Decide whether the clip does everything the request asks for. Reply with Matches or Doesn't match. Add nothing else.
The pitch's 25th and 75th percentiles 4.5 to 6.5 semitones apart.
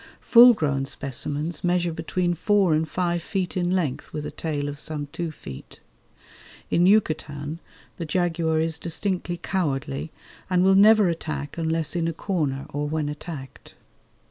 Doesn't match